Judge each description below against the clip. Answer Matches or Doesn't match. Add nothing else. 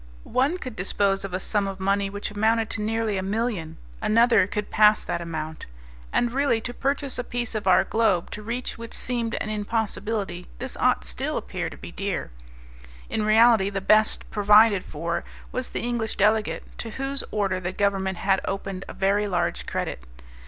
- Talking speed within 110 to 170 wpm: Doesn't match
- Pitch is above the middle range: Matches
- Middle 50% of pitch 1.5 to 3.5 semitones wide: Matches